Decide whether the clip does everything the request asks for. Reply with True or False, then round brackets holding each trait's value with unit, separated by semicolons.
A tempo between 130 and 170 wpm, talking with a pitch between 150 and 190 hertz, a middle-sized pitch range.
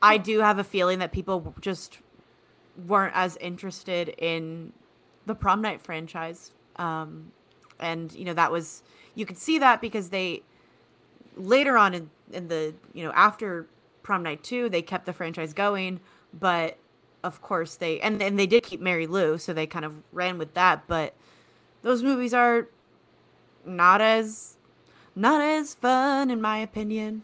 True (165 wpm; 185 Hz; 4.3 semitones)